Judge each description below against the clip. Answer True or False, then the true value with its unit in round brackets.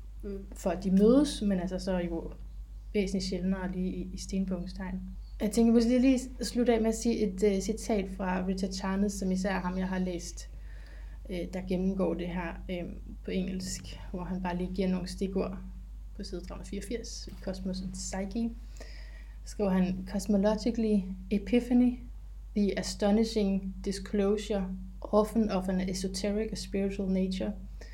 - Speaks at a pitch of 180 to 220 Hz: True (190 Hz)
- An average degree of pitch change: False (2.1 semitones)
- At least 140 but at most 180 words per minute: True (155 wpm)